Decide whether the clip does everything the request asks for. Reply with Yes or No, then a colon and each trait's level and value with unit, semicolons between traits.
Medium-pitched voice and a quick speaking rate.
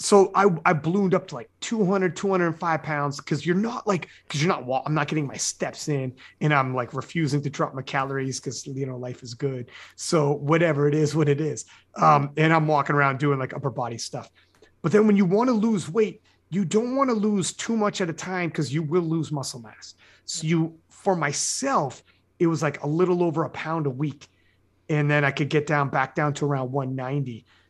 Yes: medium, 150 Hz; fast, 225 wpm